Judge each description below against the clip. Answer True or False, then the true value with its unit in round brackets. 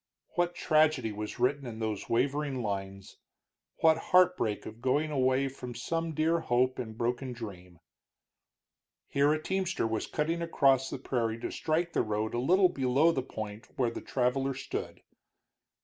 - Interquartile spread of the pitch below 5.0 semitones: False (5.3 semitones)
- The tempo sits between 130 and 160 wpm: True (155 wpm)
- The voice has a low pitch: True (130 Hz)